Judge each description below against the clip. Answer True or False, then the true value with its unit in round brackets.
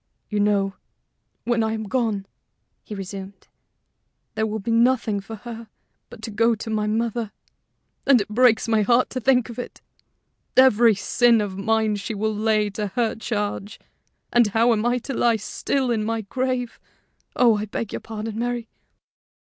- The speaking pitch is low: False (220 Hz)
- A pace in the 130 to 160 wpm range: False (170 wpm)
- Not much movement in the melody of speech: True (2.2 semitones)